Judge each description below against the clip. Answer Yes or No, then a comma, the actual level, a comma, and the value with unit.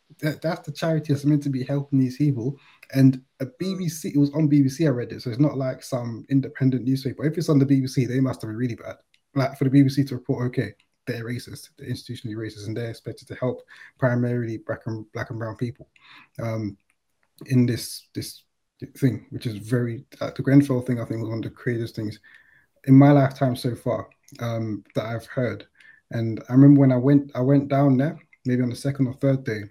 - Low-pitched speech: Yes, low, 130 Hz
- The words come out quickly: Yes, fast, 220 wpm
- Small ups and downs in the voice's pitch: No, average, 3.1 semitones